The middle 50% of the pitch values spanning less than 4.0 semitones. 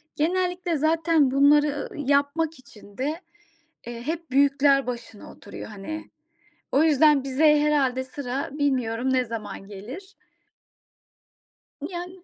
Yes: average, 3.5 semitones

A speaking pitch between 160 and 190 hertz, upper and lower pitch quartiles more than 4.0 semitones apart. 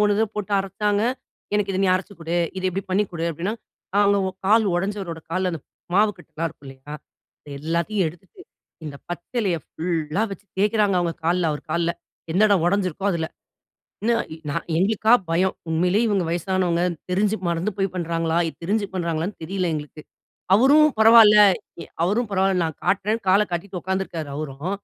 No: medium, 185 Hz; average, 3.6 semitones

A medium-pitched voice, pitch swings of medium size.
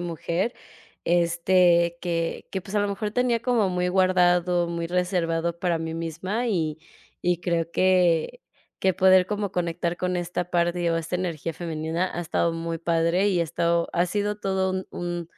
No: medium, 175 Hz; narrow, 1.9 semitones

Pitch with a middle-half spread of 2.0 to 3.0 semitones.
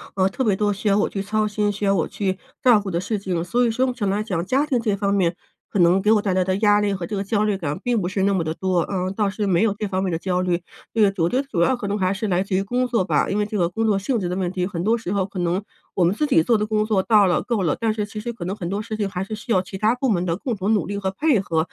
Yes: narrow, 2.6 semitones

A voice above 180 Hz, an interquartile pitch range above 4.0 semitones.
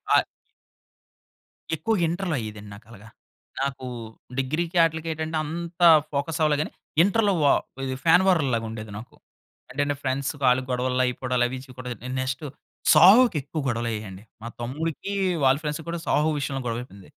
No: medium, 140 Hz; average, 4.6 semitones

